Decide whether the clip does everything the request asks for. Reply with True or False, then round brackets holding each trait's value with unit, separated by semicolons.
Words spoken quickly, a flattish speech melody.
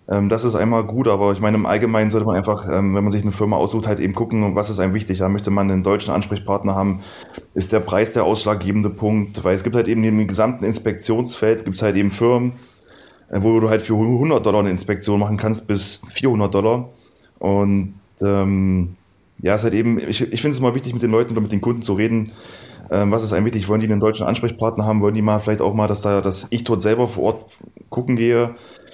True (230 wpm; 2.2 semitones)